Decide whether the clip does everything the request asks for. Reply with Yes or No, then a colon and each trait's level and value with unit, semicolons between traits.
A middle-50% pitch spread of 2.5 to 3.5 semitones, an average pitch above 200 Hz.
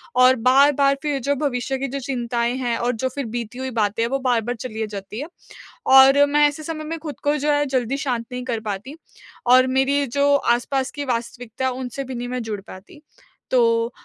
Yes: average, 2.9 semitones; very high, 255 Hz